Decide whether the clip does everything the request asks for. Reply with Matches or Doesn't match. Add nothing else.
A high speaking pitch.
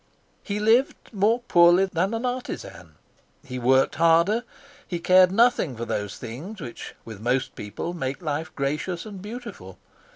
Doesn't match